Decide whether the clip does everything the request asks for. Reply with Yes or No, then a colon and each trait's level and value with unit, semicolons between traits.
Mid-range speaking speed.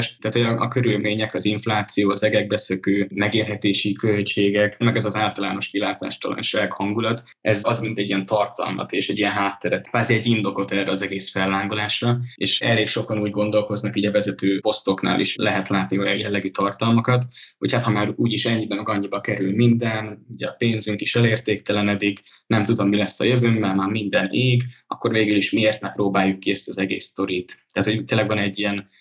No: fast, 190 wpm